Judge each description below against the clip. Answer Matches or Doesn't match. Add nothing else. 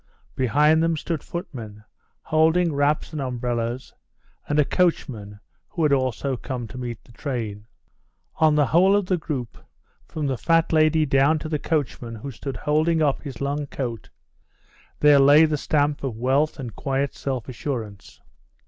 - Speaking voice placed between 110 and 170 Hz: Matches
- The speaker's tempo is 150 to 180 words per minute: Matches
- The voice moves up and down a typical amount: Matches